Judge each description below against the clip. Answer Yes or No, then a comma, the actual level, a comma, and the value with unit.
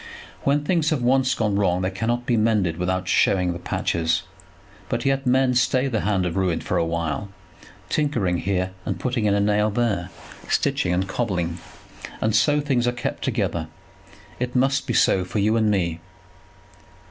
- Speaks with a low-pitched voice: Yes, low, 105 Hz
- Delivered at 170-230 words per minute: Yes, average, 175 wpm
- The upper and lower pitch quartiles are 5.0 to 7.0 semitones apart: Yes, wide, 5.4 semitones